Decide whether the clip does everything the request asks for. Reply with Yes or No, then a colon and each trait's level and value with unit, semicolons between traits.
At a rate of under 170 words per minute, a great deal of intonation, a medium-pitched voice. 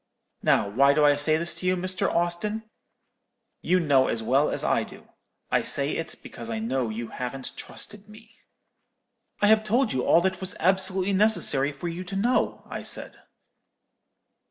No: average, 175 wpm; wide, 6.2 semitones; medium, 175 Hz